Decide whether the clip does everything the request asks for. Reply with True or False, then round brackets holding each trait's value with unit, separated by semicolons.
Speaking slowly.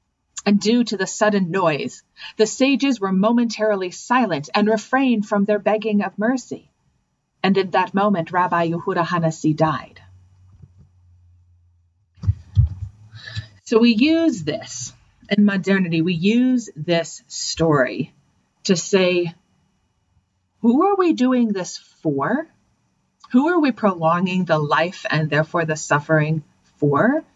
True (120 wpm)